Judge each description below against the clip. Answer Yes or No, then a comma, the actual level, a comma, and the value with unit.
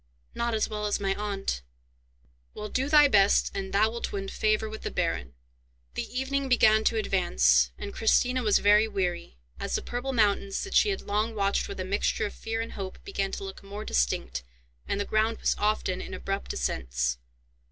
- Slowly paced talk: No, average, 195 wpm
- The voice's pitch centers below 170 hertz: No, high, 205 Hz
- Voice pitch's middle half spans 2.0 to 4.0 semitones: Yes, narrow, 2.5 semitones